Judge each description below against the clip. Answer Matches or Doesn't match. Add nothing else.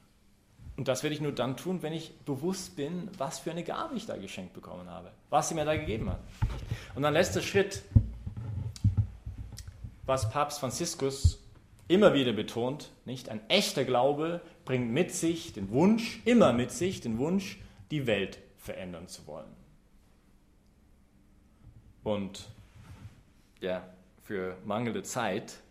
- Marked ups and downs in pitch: Matches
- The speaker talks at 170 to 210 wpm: Doesn't match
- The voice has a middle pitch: Doesn't match